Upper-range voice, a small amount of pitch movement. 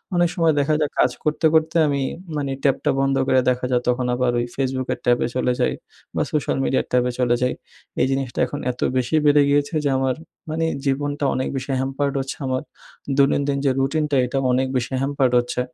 No: low, 135 Hz; narrow, 2.2 semitones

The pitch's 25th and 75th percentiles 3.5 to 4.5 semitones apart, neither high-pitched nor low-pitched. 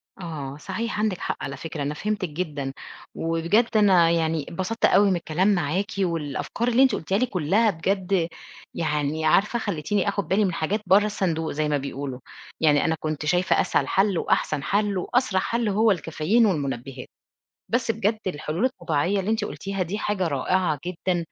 No: average, 5.0 semitones; medium, 180 Hz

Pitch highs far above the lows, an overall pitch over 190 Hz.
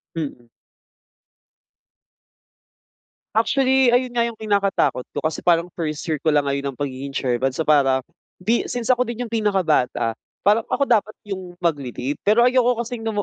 No: wide, 8.5 semitones; medium, 185 Hz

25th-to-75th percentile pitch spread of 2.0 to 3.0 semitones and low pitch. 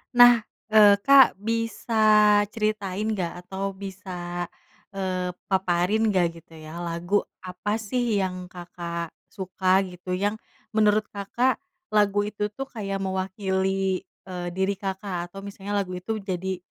No: narrow, 2.5 semitones; high, 195 Hz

